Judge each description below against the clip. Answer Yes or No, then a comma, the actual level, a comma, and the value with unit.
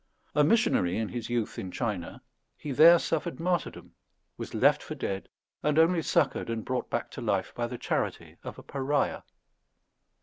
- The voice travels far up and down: Yes, wide, 6.4 semitones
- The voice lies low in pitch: Yes, low, 130 Hz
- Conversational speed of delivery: Yes, average, 170 wpm